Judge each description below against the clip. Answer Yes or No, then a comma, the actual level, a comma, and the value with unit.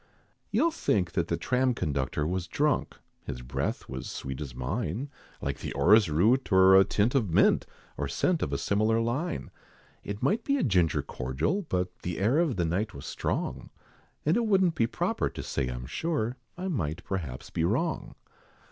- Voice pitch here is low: Yes, very low, 95 Hz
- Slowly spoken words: No, average, 180 wpm